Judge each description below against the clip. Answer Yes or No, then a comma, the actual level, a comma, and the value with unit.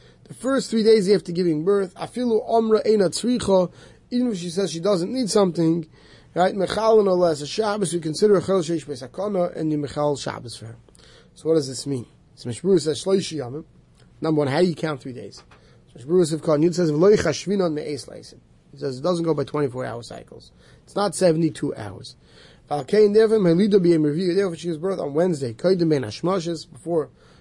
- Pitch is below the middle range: No, medium, 170 Hz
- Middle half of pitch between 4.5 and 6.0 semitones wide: Yes, average, 5.0 semitones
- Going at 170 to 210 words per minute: Yes, average, 185 wpm